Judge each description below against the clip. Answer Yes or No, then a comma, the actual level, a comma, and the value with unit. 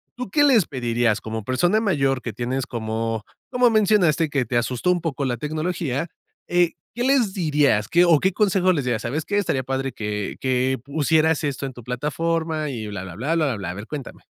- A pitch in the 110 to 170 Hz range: Yes, medium, 140 Hz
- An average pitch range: No, wide, 6.2 semitones